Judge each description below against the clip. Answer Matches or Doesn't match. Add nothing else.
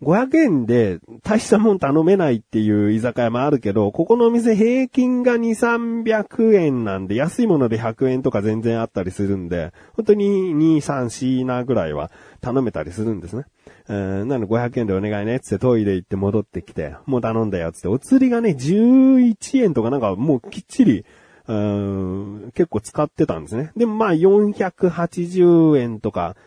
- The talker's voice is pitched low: Matches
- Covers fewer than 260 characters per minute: Doesn't match